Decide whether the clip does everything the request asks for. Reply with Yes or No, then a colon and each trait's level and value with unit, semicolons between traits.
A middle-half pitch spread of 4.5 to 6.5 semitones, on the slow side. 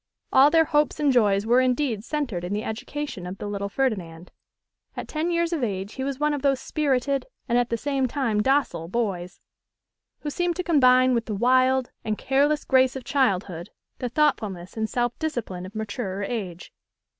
No: wide, 5.6 semitones; average, 185 wpm